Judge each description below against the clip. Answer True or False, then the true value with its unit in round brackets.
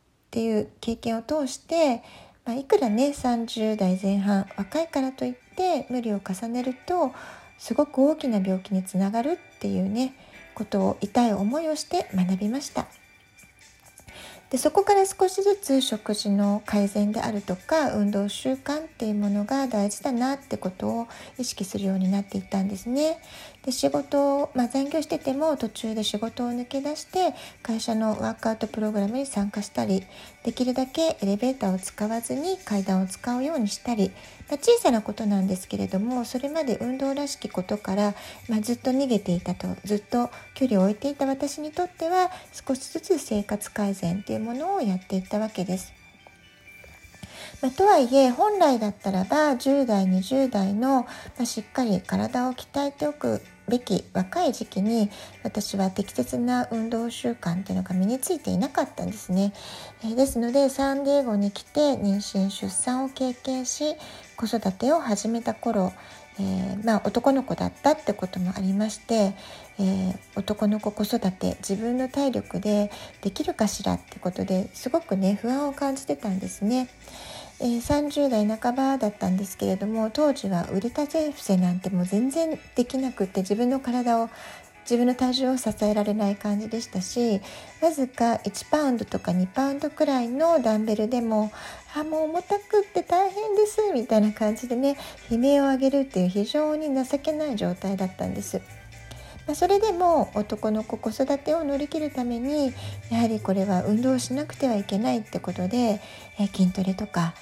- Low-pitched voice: False (230 Hz)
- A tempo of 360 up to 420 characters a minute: False (340 characters per minute)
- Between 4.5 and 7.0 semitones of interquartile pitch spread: True (5.5 semitones)